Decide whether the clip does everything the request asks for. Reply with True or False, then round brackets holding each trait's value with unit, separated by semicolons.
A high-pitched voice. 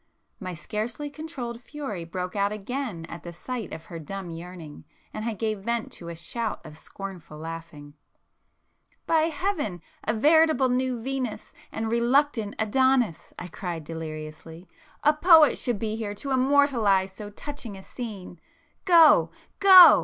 True (215 Hz)